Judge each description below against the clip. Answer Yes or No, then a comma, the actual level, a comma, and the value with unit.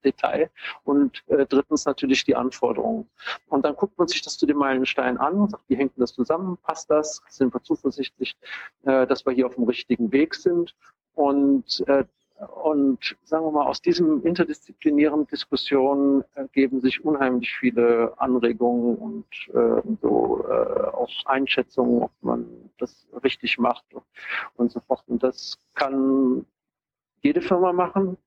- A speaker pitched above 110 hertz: Yes, medium, 140 Hz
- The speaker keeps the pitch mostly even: No, average, 5.2 semitones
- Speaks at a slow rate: No, average, 160 wpm